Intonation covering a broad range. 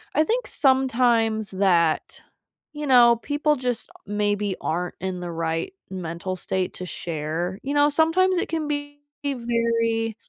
Yes: wide, 7.7 semitones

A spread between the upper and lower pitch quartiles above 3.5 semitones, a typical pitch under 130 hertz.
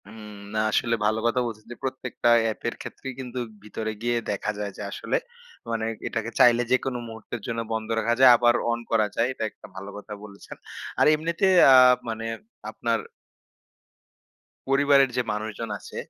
No: narrow, 2.5 semitones; low, 115 Hz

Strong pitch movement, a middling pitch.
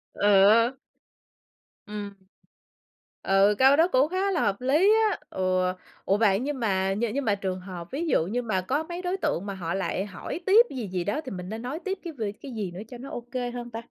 No: wide, 6.3 semitones; high, 225 Hz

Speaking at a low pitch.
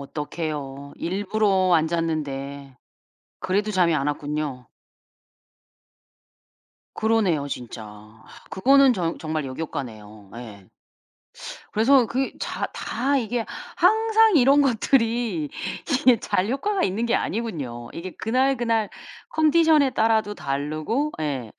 No: high, 190 Hz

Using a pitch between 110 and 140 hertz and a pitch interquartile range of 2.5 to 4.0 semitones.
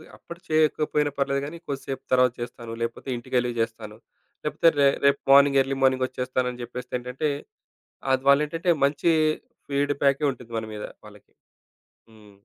Yes: low, 135 Hz; average, 2.8 semitones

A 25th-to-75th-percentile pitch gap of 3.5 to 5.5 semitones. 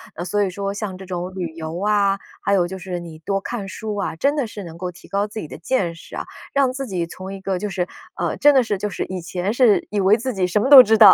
No: average, 2.8 semitones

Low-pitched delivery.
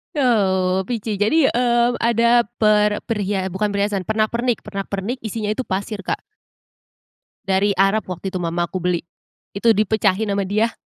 No: high, 210 Hz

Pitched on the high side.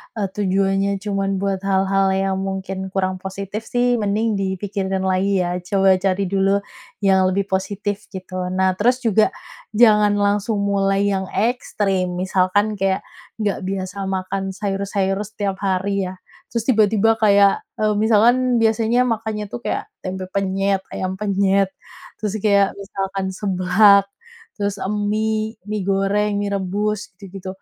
Yes: high, 195 Hz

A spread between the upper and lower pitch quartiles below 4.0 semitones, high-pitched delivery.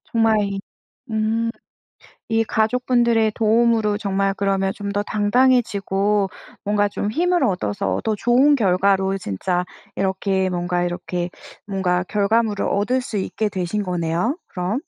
Yes: average, 2.8 semitones; high, 205 Hz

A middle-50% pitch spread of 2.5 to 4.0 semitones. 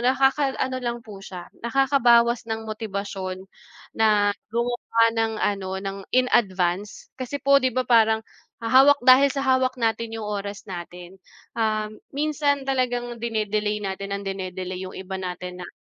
No: average, 4.5 semitones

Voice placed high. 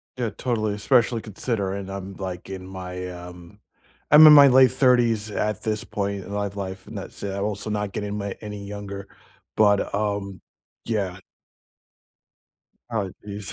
No: low, 100 Hz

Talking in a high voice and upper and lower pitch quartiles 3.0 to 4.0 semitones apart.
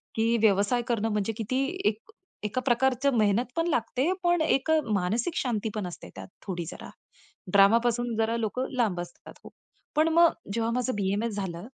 Yes: high, 230 Hz; average, 3.7 semitones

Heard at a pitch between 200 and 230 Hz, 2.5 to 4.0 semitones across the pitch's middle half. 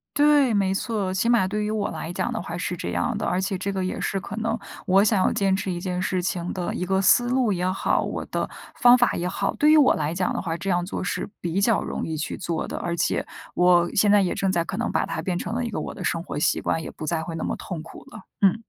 No: high, 190 Hz; average, 3.2 semitones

